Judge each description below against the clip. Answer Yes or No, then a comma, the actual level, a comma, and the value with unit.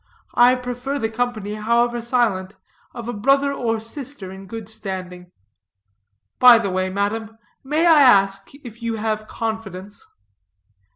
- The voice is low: No, high, 225 Hz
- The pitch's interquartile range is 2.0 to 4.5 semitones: Yes, average, 3.5 semitones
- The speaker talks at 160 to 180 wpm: No, slow, 135 wpm